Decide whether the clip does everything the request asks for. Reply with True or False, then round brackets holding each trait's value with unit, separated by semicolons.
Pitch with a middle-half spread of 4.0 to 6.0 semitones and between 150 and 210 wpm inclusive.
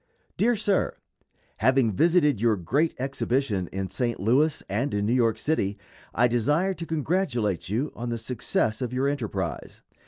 True (5.6 semitones; 160 wpm)